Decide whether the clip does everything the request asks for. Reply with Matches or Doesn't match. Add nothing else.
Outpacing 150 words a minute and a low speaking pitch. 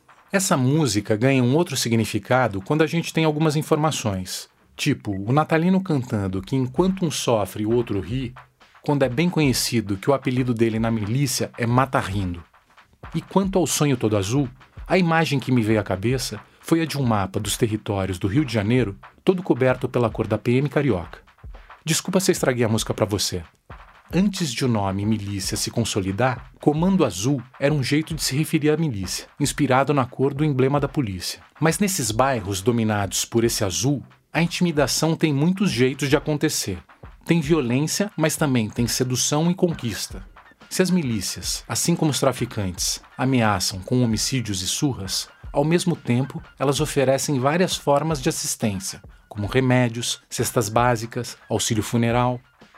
Matches